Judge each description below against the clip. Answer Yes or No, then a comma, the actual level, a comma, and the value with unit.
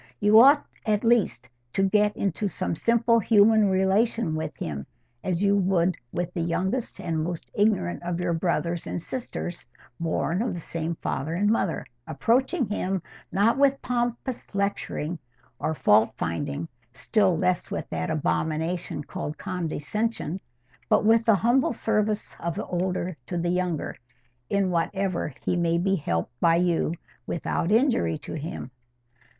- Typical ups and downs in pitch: Yes, average, 4.4 semitones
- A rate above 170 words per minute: No, average, 150 wpm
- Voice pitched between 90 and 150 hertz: No, medium, 180 Hz